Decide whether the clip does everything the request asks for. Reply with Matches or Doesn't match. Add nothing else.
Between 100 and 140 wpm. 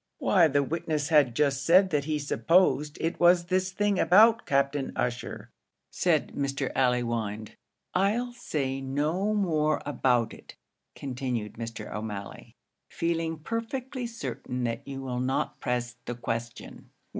Matches